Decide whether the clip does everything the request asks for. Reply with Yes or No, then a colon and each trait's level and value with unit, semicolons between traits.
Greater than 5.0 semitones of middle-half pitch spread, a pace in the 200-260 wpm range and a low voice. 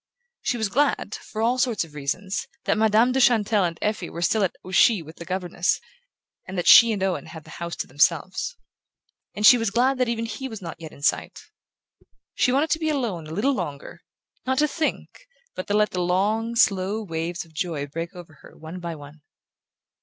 No: wide, 5.5 semitones; fast, 205 wpm; high, 195 Hz